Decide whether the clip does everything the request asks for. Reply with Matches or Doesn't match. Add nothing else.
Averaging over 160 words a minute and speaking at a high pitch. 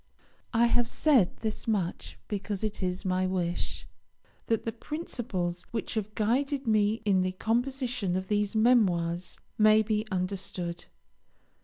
Doesn't match